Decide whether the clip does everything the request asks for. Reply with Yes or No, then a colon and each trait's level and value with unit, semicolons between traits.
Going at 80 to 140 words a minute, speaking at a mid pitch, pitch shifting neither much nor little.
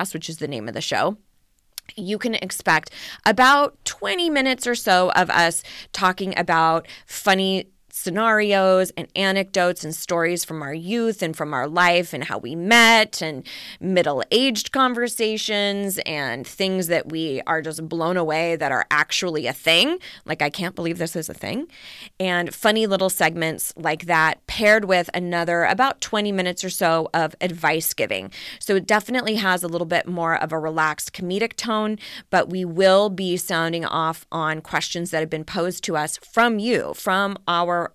No: average, 170 wpm; medium, 180 Hz; average, 4.3 semitones